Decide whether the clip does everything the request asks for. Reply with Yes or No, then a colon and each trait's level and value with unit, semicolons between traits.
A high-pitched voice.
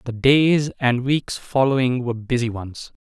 No: low, 125 Hz